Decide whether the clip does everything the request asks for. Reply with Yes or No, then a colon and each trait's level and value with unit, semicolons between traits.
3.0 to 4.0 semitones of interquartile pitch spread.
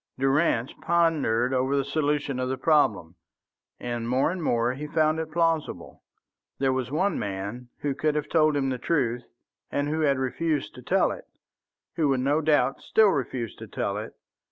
Yes: average, 3.6 semitones